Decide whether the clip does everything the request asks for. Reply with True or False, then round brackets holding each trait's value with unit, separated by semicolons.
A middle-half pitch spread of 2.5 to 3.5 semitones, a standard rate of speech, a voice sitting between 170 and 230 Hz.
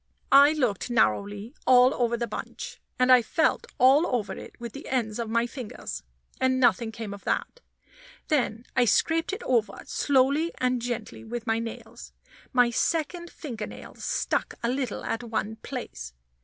False (2.9 semitones; 165 wpm; 240 Hz)